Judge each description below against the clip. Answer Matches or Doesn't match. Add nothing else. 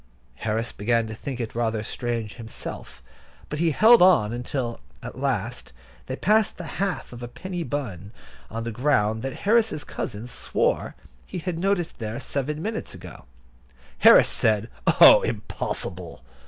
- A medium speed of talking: Matches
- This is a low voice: Matches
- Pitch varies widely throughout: Matches